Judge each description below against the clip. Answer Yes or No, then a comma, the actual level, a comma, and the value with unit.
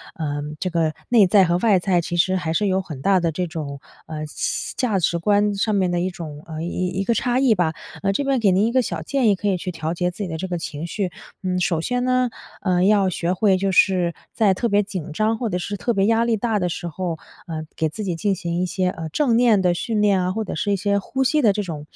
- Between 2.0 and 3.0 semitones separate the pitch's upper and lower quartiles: No, average, 3.5 semitones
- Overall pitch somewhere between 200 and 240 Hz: No, medium, 185 Hz